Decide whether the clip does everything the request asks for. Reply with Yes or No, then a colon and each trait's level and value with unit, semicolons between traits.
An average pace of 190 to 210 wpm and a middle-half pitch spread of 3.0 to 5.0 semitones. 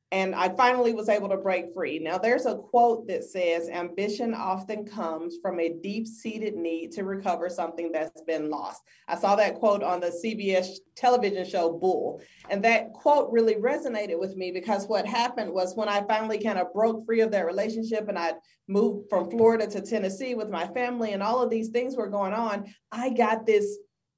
Yes: average, 200 wpm; average, 3.7 semitones